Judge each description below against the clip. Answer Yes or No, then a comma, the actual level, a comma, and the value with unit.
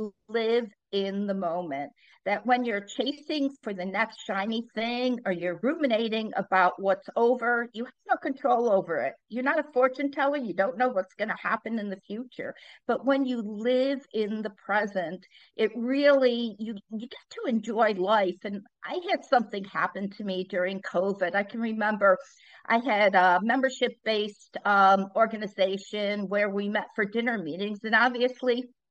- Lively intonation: No, average, 4.0 semitones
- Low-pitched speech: No, high, 220 Hz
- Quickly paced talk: No, average, 170 wpm